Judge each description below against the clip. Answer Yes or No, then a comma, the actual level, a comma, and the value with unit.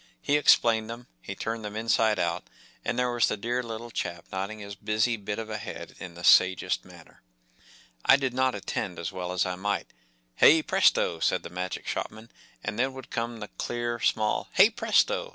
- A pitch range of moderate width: Yes, average, 3.9 semitones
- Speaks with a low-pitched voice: Yes, low, 110 Hz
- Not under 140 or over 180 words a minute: No, fast, 205 wpm